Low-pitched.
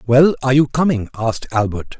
Yes: low, 125 Hz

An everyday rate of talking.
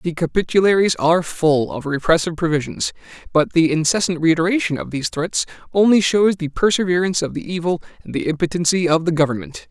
Yes: average, 165 wpm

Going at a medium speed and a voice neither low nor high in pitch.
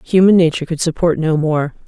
Yes: average, 190 wpm; medium, 165 Hz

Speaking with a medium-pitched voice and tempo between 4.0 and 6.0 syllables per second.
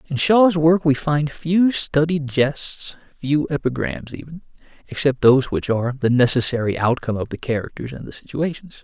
Yes: medium, 145 Hz; 5.0 syllables/s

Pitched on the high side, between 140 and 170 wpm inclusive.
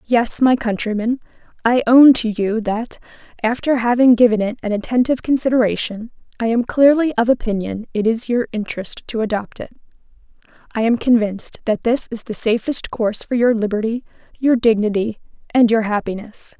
Yes: high, 230 Hz; average, 160 wpm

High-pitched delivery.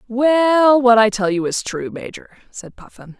Yes: high, 230 Hz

